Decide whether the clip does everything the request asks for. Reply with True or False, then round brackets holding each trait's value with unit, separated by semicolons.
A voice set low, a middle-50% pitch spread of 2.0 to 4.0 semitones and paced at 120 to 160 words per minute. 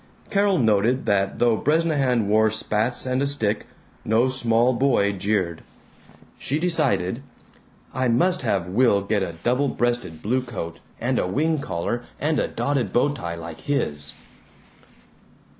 False (120 Hz; 5.4 semitones; 140 wpm)